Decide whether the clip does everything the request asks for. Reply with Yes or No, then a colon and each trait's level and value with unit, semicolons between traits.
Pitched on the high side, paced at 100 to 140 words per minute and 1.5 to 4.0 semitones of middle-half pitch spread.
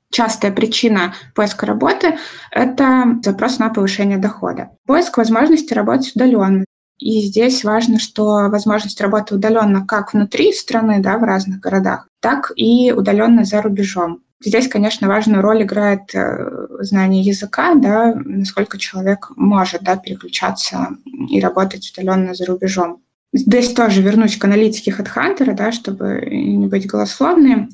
Yes: high, 210 Hz; average, 130 wpm; average, 2.9 semitones